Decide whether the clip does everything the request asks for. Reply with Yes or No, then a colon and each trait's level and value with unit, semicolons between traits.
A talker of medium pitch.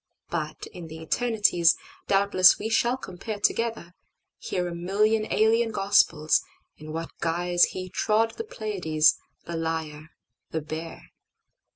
Yes: medium, 180 Hz